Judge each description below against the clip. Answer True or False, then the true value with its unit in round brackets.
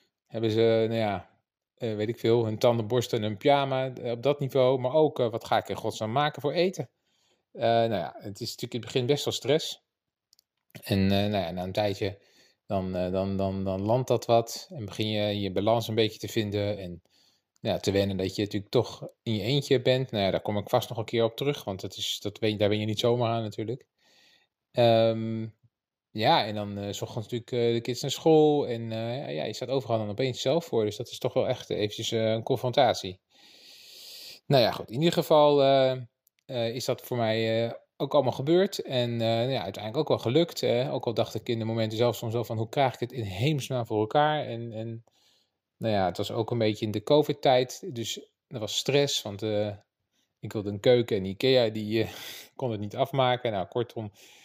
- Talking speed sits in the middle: False (225 wpm)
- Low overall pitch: True (115 Hz)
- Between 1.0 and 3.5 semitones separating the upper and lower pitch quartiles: True (3.2 semitones)